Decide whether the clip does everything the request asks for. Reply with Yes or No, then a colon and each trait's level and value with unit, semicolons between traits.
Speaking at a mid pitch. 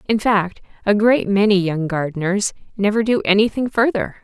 No: high, 205 Hz